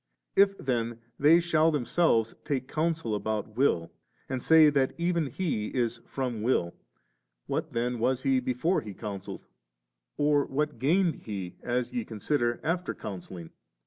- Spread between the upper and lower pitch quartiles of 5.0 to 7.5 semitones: Yes, wide, 5.6 semitones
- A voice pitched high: No, low, 130 Hz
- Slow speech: No, average, 145 wpm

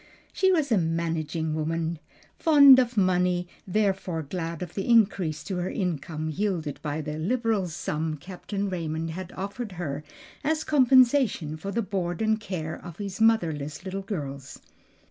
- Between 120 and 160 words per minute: Yes, average, 150 wpm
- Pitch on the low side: No, medium, 180 Hz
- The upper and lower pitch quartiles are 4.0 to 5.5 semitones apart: Yes, average, 4.9 semitones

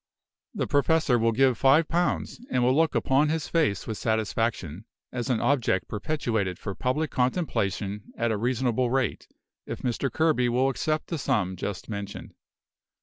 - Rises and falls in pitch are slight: No, average, 4.6 semitones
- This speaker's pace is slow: No, average, 155 wpm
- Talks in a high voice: No, low, 125 Hz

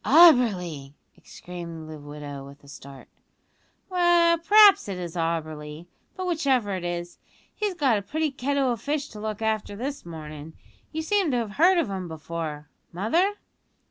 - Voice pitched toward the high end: Yes, high, 205 Hz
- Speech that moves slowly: No, average, 160 wpm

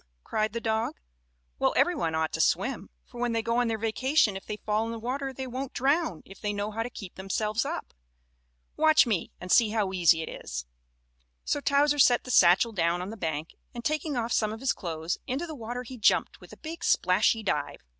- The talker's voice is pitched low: No, high, 225 Hz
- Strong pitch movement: No, average, 4.9 semitones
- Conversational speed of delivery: No, fast, 225 wpm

